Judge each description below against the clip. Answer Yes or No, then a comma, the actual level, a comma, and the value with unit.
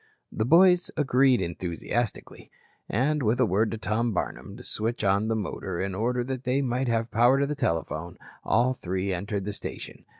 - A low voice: Yes, low, 115 Hz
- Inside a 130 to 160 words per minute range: No, average, 175 wpm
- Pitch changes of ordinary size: Yes, average, 4.4 semitones